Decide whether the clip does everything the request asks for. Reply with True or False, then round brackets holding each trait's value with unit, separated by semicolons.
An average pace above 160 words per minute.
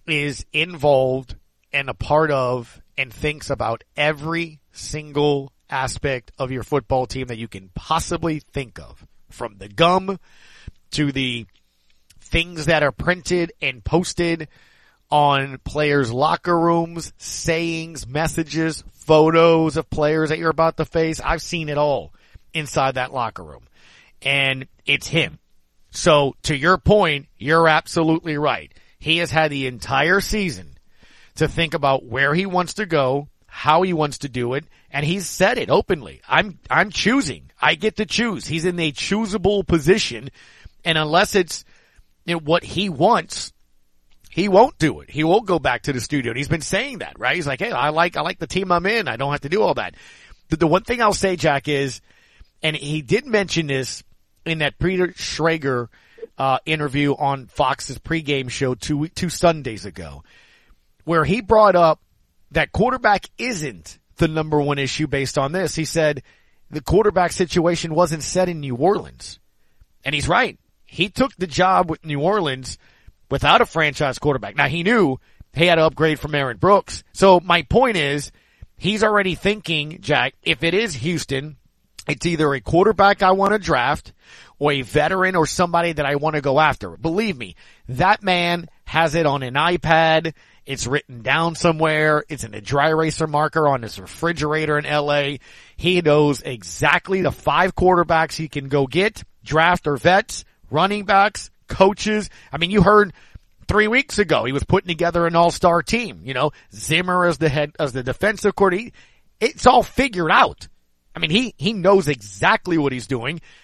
True (170 wpm)